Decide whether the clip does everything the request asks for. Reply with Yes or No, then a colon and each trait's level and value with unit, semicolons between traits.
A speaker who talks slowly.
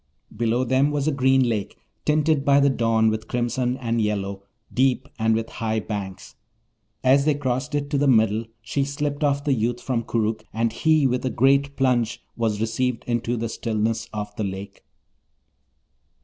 No: average, 175 wpm